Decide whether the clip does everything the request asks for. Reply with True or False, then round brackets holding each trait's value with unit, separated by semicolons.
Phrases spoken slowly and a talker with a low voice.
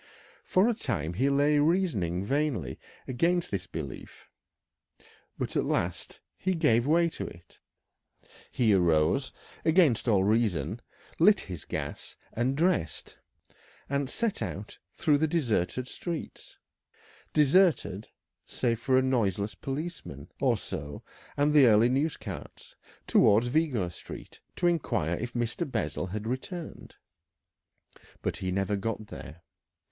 True (125 wpm; 125 Hz)